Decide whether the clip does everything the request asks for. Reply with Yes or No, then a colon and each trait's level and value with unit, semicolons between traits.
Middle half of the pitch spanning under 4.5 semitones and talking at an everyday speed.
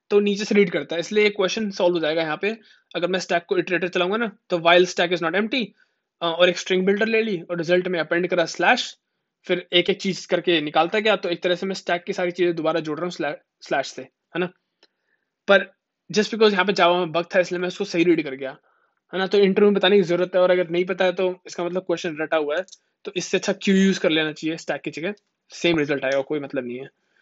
No: narrow, 2.4 semitones; fast, 260 wpm